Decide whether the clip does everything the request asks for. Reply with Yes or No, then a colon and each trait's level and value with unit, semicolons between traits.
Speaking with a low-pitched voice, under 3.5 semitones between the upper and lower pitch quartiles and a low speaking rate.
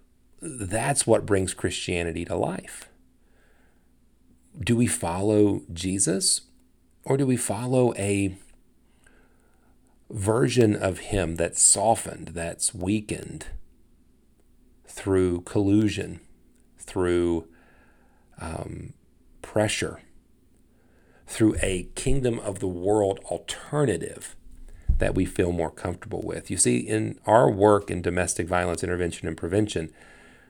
No: very low, 95 Hz; average, 3.8 semitones; slow, 100 wpm